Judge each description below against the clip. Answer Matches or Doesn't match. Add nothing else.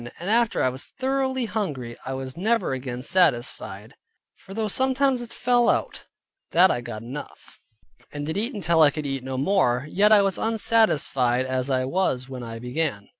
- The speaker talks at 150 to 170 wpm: Doesn't match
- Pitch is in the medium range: Matches